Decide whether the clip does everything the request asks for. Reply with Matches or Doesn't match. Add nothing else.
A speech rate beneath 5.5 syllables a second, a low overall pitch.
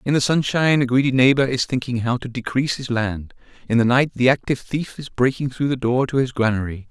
Doesn't match